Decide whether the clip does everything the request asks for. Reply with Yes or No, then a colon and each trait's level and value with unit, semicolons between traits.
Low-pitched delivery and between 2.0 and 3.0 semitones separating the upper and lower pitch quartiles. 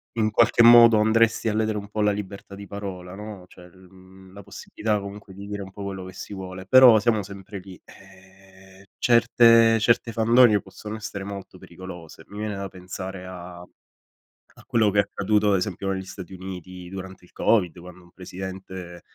Yes: low, 100 Hz; narrow, 2.4 semitones